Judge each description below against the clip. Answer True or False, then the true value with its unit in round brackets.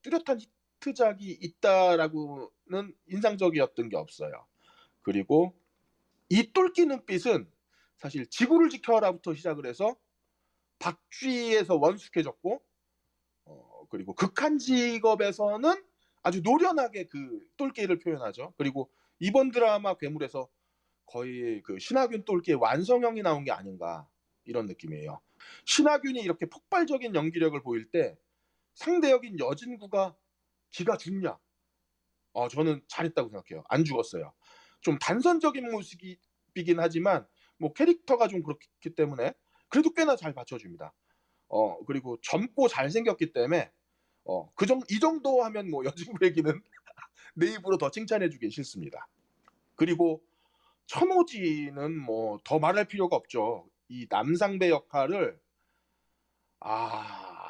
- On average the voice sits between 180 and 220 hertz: True (190 Hz)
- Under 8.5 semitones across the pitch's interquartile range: False (8.9 semitones)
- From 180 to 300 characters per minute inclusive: True (275 characters per minute)